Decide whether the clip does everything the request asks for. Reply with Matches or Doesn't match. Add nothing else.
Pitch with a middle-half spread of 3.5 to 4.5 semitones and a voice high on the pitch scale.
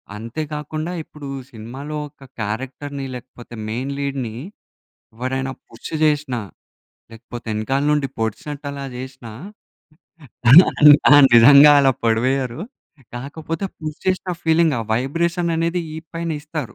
Doesn't match